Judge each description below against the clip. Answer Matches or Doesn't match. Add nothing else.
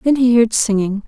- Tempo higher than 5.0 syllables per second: Doesn't match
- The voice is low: Doesn't match